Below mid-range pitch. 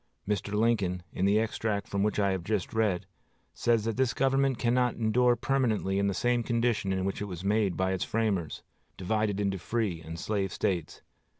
Yes: low, 105 Hz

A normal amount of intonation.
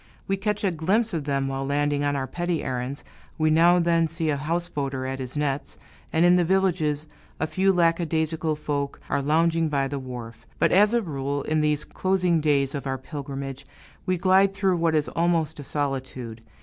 Yes: average, 3.8 semitones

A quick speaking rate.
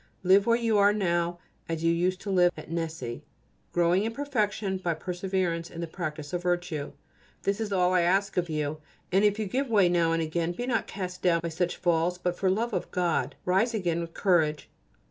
Yes: fast, 210 wpm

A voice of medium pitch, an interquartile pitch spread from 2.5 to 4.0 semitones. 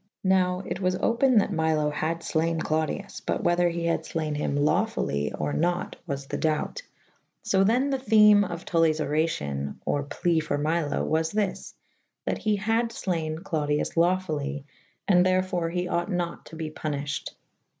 Yes: medium, 170 Hz; average, 3.3 semitones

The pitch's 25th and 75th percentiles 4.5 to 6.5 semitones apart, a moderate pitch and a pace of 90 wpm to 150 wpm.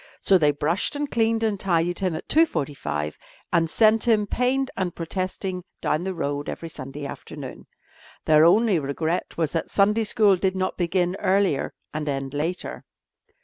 No: average, 4.9 semitones; medium, 180 Hz; average, 160 wpm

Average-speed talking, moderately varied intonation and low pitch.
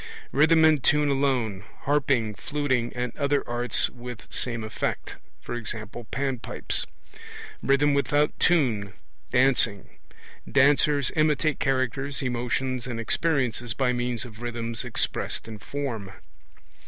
No: slow, 110 wpm; average, 3.2 semitones; low, 130 Hz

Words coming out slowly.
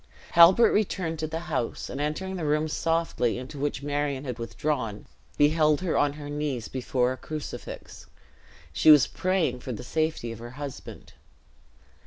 No: average, 160 wpm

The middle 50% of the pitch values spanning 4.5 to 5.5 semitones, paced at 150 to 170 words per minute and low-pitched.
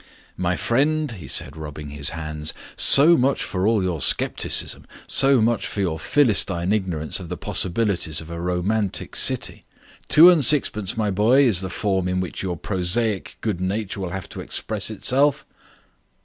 Yes: average, 4.9 semitones; average, 165 wpm; very low, 95 Hz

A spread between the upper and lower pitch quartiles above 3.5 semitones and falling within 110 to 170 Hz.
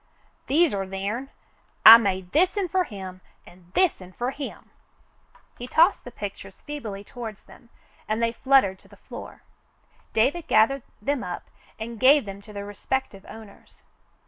No: wide, 5.6 semitones; high, 225 Hz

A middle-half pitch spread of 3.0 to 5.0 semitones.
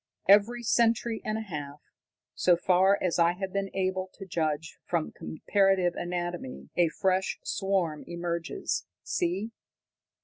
No: narrow, 2.5 semitones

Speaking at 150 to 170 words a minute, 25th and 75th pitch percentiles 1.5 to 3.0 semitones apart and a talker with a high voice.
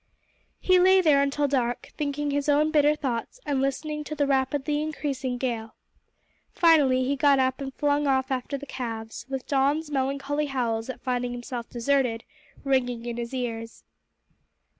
Yes: average, 160 wpm; average, 2.7 semitones; very high, 270 Hz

